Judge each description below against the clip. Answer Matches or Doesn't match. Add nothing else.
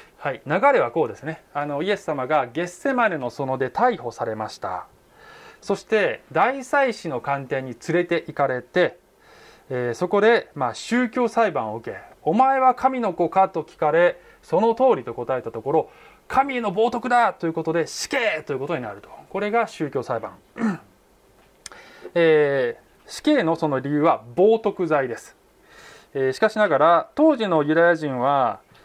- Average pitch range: Doesn't match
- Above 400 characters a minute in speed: Doesn't match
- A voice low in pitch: Doesn't match